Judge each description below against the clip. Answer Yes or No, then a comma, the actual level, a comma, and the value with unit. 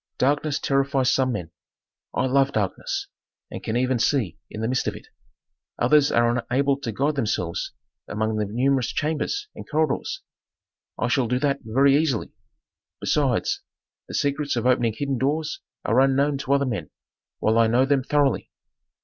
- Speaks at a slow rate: No, average, 160 wpm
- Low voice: Yes, low, 130 Hz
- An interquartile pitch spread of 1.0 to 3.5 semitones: Yes, average, 3.1 semitones